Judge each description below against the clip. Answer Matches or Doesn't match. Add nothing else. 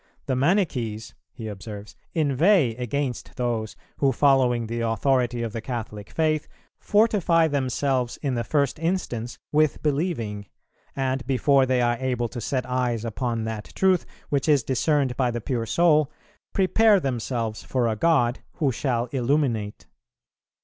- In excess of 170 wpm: Doesn't match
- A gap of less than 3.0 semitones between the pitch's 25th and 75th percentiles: Doesn't match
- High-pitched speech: Doesn't match